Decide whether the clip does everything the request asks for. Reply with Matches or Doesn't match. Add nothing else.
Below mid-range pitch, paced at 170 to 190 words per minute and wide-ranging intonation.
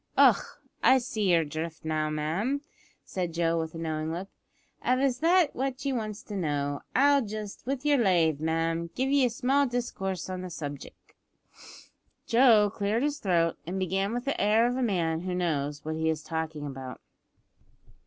Doesn't match